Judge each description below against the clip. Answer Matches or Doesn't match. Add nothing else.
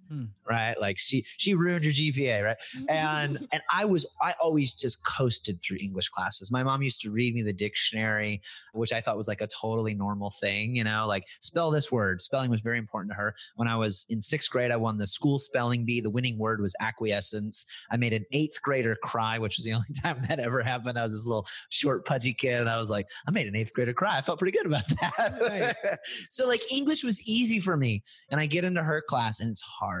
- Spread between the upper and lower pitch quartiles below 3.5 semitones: Doesn't match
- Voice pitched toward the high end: Doesn't match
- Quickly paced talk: Matches